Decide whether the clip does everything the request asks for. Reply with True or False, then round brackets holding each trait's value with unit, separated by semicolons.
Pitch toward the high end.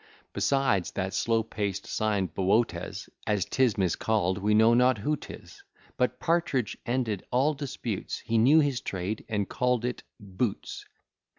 False (110 Hz)